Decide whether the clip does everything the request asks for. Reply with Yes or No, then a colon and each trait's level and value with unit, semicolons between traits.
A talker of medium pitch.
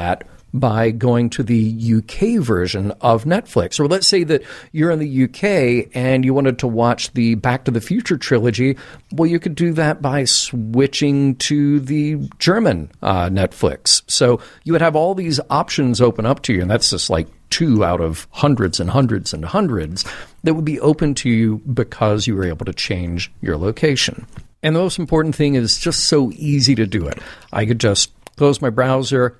No: low, 130 Hz